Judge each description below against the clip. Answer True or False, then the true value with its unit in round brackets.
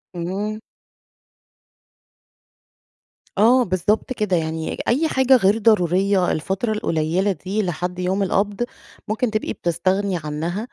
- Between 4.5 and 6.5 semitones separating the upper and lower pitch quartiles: False (3.4 semitones)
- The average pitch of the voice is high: True (195 Hz)